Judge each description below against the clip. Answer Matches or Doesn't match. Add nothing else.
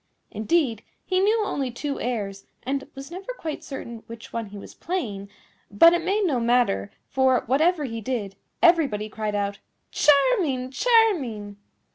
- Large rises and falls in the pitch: Matches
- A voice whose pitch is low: Doesn't match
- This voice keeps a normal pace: Matches